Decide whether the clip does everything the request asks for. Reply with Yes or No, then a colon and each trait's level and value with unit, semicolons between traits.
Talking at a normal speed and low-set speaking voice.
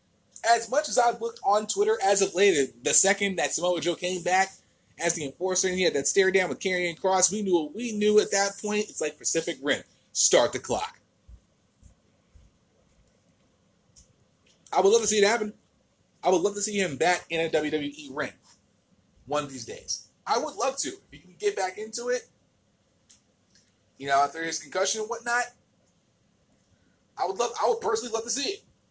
No: average, 195 wpm; high, 195 Hz